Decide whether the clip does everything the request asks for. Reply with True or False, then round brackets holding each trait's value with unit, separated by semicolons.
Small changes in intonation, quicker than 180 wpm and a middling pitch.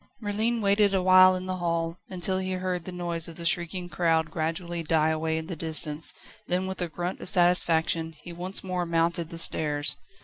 True (2.2 semitones; 200 wpm; 175 Hz)